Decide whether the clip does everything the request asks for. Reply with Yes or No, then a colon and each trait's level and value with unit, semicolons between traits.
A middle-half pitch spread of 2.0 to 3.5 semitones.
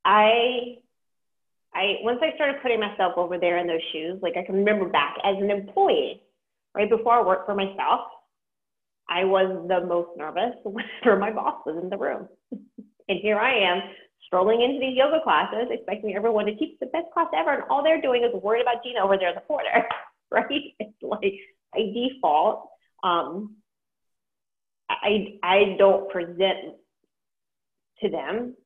No: average, 4.7 semitones